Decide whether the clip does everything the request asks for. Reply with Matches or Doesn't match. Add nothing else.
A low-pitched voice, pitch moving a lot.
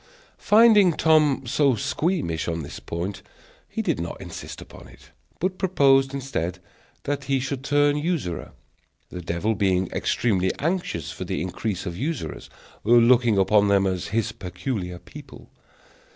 Matches